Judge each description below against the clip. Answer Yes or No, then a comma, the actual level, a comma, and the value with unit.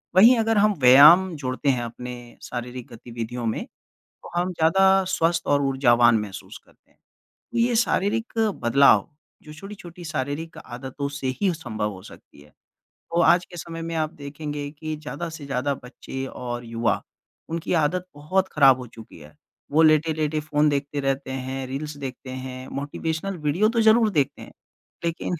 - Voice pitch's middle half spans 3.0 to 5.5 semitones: Yes, average, 4.7 semitones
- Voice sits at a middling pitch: Yes, medium, 145 Hz